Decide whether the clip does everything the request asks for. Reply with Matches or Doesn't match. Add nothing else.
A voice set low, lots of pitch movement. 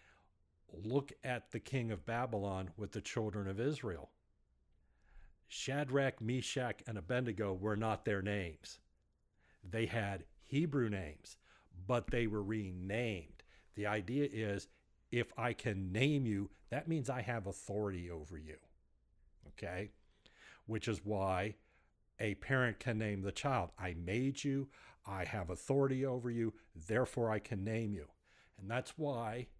Doesn't match